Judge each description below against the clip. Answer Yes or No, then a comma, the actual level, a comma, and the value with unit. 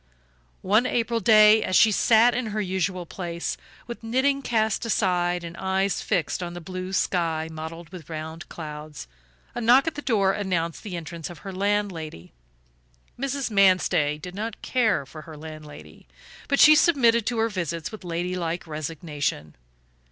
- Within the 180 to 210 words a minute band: No, average, 160 wpm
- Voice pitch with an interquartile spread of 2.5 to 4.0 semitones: No, average, 5.2 semitones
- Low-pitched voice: No, medium, 185 Hz